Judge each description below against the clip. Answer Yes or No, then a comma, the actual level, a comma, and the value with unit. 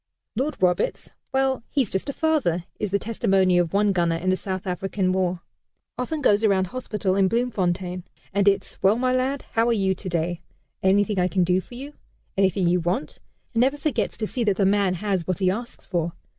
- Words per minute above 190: Yes, average, 200 wpm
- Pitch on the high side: Yes, high, 195 Hz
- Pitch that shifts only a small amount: No, average, 4.0 semitones